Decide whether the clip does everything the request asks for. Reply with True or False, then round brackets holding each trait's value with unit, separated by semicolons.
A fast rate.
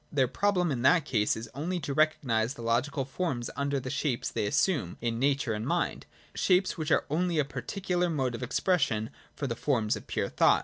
True (210 wpm)